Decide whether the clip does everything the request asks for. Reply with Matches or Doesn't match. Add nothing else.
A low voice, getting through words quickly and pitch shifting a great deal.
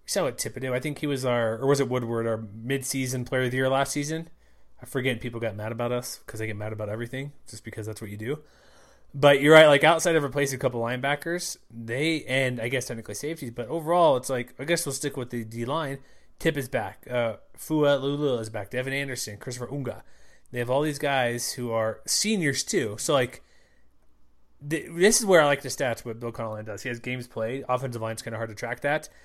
Doesn't match